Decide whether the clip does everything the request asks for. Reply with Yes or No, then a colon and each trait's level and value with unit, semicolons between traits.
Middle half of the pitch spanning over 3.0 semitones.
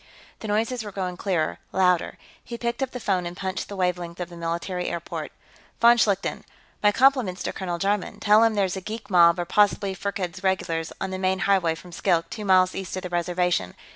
No: narrow, 2.6 semitones